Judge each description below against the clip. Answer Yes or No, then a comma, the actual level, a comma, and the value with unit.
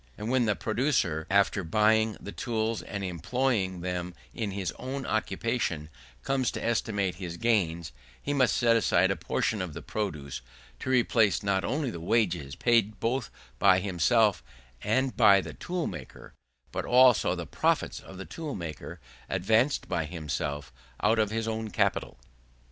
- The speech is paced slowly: No, average, 160 wpm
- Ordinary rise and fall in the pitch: Yes, average, 4.5 semitones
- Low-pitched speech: Yes, low, 105 Hz